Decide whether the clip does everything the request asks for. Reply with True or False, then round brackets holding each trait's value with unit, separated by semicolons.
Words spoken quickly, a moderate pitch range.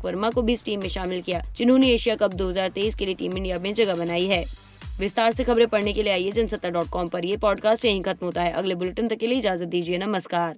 True (250 wpm; 3.7 semitones)